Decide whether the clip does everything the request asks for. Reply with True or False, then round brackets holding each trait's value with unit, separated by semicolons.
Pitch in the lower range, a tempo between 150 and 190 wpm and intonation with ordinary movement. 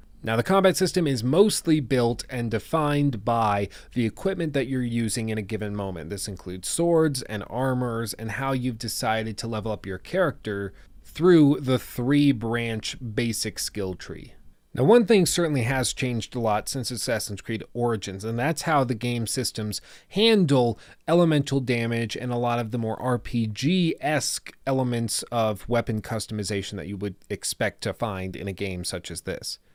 True (120 Hz; 170 wpm; 4.4 semitones)